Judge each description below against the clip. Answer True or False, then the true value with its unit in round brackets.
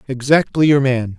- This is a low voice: True (130 Hz)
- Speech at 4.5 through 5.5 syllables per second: True (4.9 syllables/s)